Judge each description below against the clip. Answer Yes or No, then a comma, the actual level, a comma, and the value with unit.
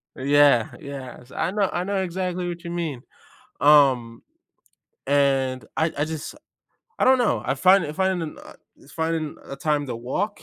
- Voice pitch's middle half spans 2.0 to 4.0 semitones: No, average, 4.7 semitones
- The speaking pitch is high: No, medium, 150 Hz